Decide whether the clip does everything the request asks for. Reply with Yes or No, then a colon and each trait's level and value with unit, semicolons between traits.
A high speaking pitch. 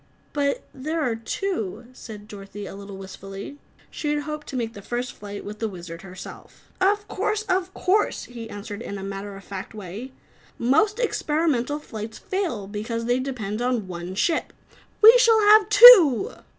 Yes: high, 235 Hz